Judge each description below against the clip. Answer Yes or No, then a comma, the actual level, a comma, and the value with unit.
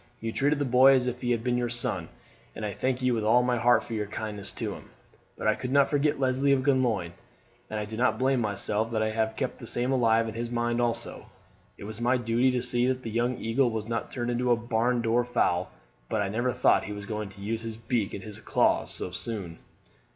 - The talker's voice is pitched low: Yes, low, 120 Hz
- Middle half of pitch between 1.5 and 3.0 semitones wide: Yes, narrow, 2.4 semitones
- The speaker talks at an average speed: No, fast, 245 wpm